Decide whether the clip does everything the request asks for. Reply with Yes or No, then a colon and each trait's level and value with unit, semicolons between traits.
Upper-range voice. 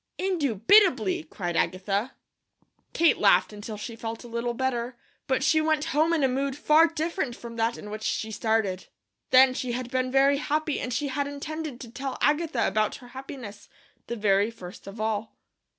Yes: very high, 250 Hz